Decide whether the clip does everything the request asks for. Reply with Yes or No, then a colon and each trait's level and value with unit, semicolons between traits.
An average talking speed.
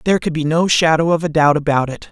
No: fast, 285 wpm